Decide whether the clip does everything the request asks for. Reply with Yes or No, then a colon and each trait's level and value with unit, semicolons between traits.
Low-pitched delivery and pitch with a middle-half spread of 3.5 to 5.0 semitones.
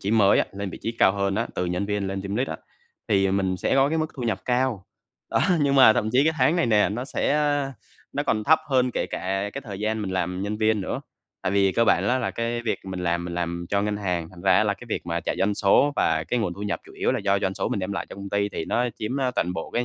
Yes: low, 100 Hz; average, 4.0 semitones